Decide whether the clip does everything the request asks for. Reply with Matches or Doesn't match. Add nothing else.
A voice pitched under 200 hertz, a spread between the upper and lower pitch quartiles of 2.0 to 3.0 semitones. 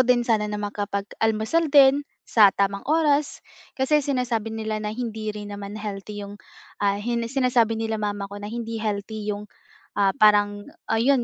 Doesn't match